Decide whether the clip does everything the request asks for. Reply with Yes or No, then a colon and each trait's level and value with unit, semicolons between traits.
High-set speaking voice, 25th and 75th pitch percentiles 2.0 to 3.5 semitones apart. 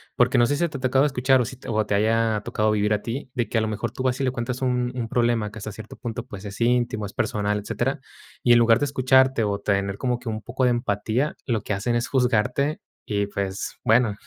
No: low, 120 Hz; average, 3.0 semitones